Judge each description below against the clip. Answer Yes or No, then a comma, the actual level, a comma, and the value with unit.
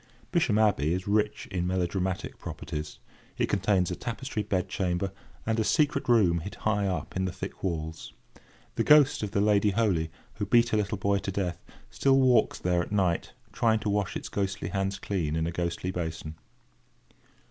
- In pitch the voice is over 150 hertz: No, low, 100 Hz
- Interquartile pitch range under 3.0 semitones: No, average, 3.3 semitones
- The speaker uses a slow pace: No, average, 180 wpm